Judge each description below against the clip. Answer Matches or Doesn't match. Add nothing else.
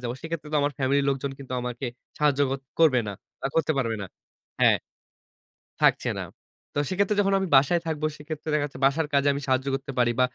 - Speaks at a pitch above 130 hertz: Matches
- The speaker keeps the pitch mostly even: Doesn't match